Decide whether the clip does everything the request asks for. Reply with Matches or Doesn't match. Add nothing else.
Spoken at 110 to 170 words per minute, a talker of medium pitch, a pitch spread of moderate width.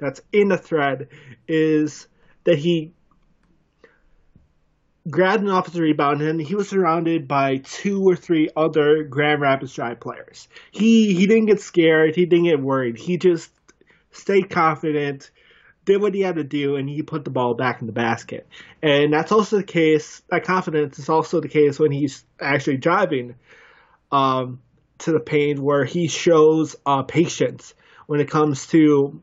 Matches